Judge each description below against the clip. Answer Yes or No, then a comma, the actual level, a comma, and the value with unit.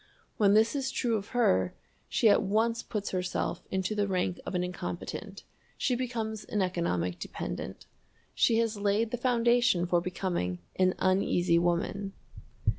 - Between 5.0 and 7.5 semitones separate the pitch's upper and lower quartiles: No, average, 4.0 semitones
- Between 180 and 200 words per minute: No, average, 150 wpm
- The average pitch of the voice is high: Yes, high, 200 Hz